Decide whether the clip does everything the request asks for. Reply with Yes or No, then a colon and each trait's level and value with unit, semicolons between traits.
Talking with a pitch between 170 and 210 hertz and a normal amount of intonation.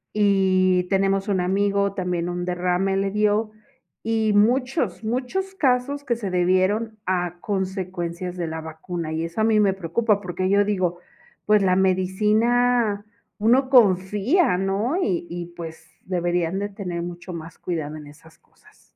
Yes: high, 190 Hz; average, 3.2 semitones